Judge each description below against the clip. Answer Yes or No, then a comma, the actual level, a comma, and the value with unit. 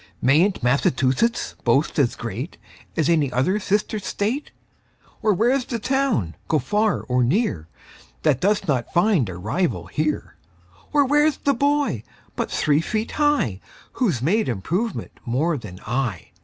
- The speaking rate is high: No, average, 140 wpm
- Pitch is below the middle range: No, medium, 170 Hz